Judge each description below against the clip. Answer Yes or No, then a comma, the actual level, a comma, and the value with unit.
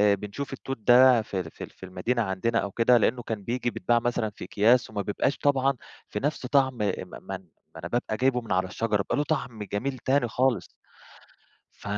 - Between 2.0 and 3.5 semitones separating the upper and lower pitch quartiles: No, average, 4.1 semitones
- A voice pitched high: No, low, 115 Hz